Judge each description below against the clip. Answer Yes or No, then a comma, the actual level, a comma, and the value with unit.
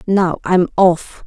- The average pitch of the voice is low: No, medium, 180 Hz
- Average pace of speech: Yes, average, 190 wpm